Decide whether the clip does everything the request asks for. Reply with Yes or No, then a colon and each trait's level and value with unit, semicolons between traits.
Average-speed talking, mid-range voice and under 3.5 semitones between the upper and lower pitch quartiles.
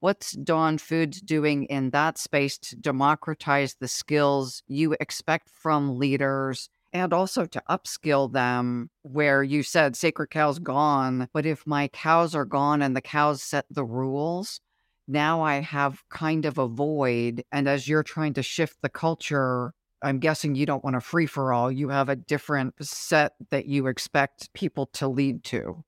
Yes: average, 170 wpm; medium, 145 Hz; narrow, 2.4 semitones